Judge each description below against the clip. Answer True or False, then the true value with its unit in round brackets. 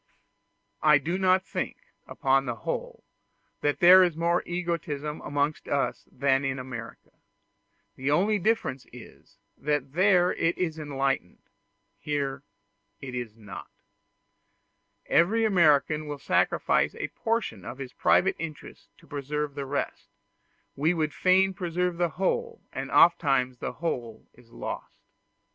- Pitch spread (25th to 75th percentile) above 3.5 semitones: True (4.6 semitones)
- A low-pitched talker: False (150 Hz)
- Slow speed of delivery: True (130 wpm)